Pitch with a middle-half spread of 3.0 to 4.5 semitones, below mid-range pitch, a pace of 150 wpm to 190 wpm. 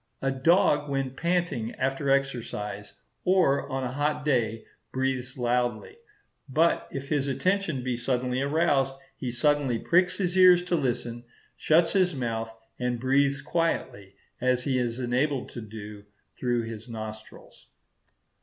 No: average, 3.7 semitones; low, 130 Hz; slow, 135 wpm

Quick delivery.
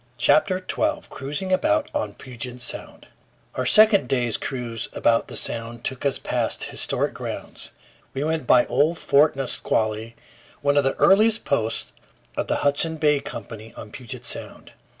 No: average, 155 wpm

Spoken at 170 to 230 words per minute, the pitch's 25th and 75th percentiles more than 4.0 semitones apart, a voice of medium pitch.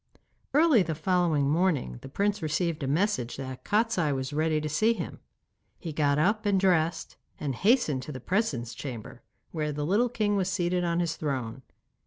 Yes: average, 180 wpm; wide, 5.4 semitones; medium, 160 Hz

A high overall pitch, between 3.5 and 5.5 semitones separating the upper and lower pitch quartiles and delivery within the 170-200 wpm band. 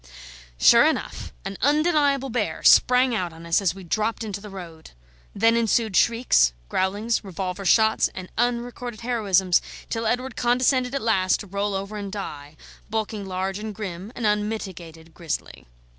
No: high, 210 Hz; average, 4.0 semitones; average, 155 wpm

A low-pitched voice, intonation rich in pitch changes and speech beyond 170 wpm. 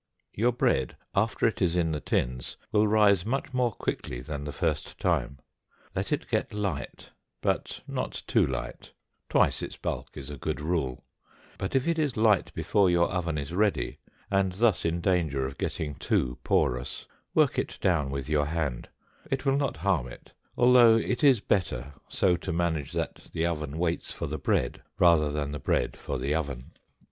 Yes: very low, 85 Hz; wide, 6.3 semitones; average, 180 wpm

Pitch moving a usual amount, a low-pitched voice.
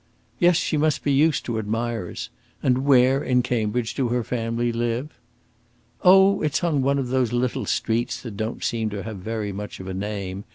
Yes: average, 3.6 semitones; low, 120 Hz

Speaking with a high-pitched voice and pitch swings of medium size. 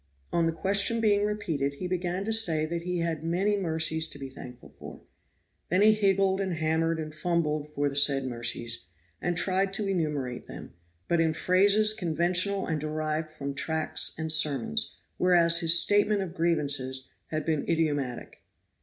No: medium, 165 Hz; average, 3.8 semitones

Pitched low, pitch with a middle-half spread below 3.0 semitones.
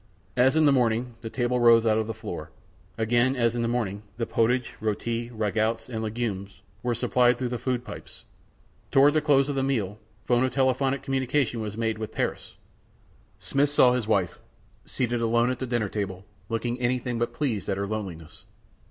Yes: low, 120 Hz; narrow, 2.6 semitones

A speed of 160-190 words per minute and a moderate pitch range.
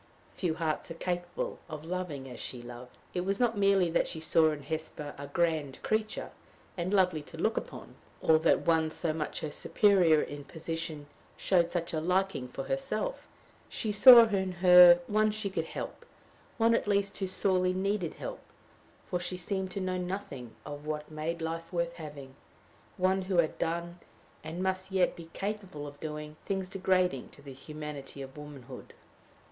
Yes: average, 175 wpm; average, 3.9 semitones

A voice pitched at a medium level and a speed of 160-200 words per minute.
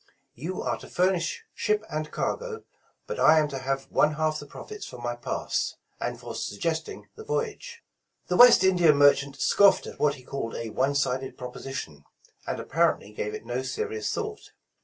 Yes: medium, 145 Hz; average, 180 wpm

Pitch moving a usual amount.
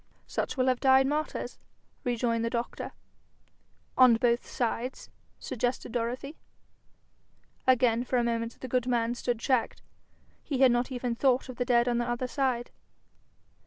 No: narrow, 1.5 semitones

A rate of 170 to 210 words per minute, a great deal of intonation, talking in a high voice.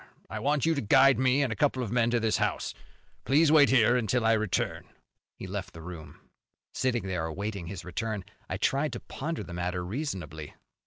No: average, 200 wpm; wide, 6.6 semitones; low, 115 Hz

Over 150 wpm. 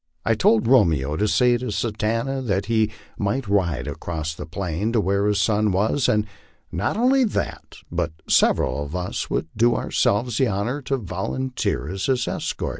Yes: average, 180 wpm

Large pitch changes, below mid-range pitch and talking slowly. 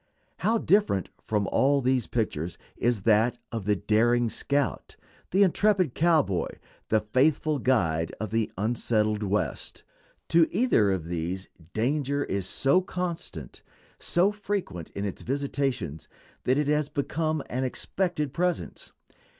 Yes: wide, 7.0 semitones; low, 125 Hz; slow, 130 wpm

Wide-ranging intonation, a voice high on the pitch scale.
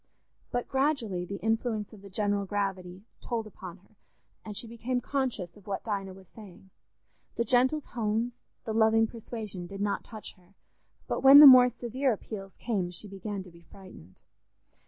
No: average, 3.5 semitones; high, 210 Hz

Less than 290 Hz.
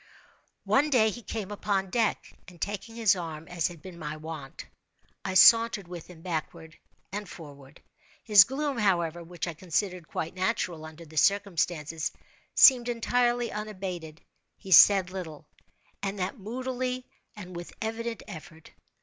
Yes: medium, 185 Hz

